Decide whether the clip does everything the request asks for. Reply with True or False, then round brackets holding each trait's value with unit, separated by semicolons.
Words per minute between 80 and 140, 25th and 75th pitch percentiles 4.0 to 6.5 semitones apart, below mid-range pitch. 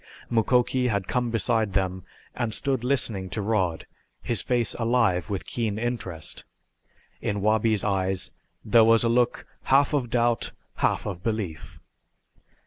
False (135 wpm; 3.6 semitones; 110 Hz)